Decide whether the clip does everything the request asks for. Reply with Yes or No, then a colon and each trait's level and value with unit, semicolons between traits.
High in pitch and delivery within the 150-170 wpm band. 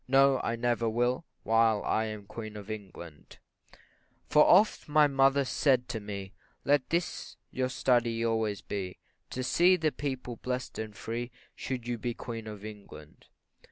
No: low, 115 Hz; average, 155 wpm